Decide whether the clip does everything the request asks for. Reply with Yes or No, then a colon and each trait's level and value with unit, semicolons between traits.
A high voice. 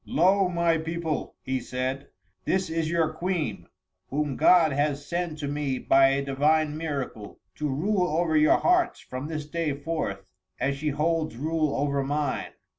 No: medium, 150 Hz